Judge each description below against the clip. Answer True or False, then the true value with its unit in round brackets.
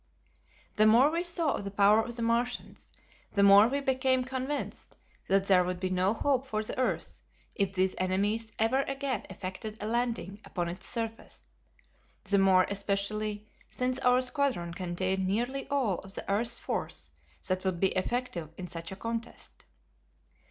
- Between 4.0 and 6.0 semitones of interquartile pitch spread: True (4.7 semitones)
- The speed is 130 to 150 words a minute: False (165 wpm)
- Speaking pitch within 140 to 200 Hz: False (215 Hz)